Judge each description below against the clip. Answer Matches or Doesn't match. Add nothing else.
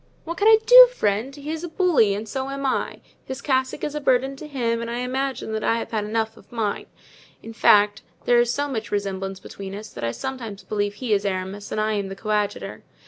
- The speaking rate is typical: Doesn't match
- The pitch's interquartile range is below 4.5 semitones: Doesn't match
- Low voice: Doesn't match